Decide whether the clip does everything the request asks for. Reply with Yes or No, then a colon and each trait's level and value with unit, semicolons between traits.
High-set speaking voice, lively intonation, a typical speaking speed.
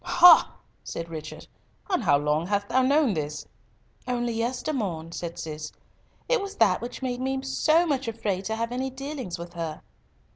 Yes: high, 230 Hz; wide, 7.9 semitones; average, 170 wpm